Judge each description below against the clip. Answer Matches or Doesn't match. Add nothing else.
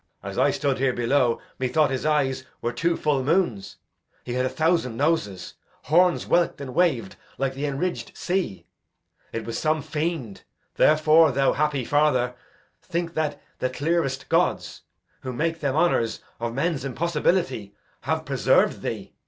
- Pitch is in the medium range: Matches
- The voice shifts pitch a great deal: Doesn't match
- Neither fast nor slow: Matches